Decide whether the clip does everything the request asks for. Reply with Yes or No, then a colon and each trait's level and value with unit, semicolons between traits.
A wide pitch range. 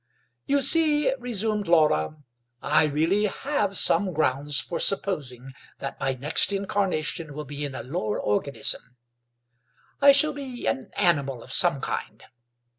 Yes: wide, 7.6 semitones